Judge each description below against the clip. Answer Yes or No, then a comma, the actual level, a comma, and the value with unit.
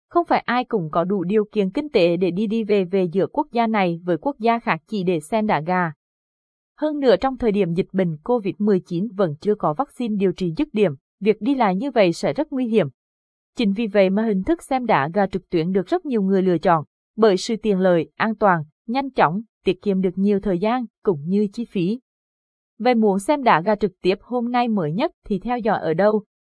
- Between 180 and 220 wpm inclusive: No, average, 235 wpm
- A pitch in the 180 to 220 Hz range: Yes, high, 205 Hz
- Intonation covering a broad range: No, average, 4.0 semitones